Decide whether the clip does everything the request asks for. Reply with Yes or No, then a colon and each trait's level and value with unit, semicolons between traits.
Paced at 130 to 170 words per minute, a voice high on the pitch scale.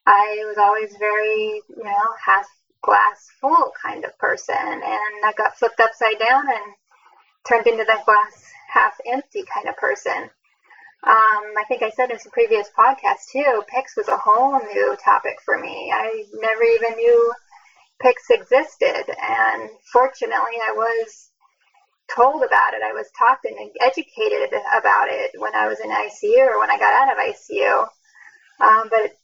Yes: average, 165 wpm; very high, 260 Hz